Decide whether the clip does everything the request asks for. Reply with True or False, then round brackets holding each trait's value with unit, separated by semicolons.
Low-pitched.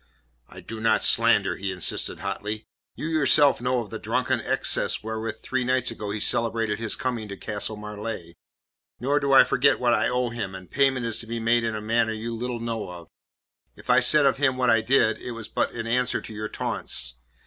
True (115 Hz)